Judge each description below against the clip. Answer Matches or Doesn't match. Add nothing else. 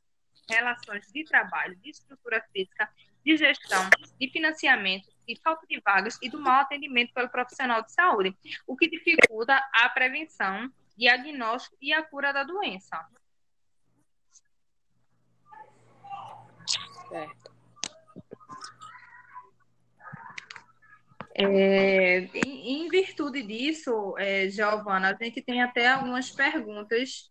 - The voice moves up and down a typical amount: Doesn't match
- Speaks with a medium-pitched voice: Doesn't match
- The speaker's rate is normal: Doesn't match